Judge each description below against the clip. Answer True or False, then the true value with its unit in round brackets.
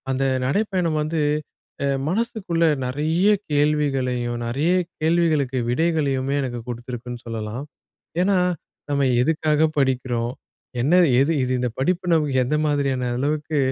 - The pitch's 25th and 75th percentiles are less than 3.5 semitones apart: False (4.1 semitones)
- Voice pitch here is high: False (140 Hz)